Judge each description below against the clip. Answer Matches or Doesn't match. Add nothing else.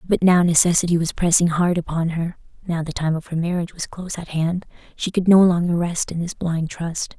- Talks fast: Matches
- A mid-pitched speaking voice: Matches